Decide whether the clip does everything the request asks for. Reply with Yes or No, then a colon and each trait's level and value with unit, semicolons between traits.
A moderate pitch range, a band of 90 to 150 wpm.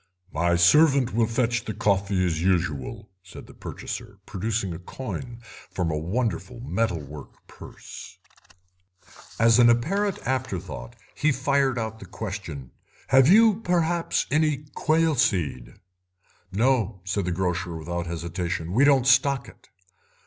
No: wide, 7.1 semitones; slow, 135 wpm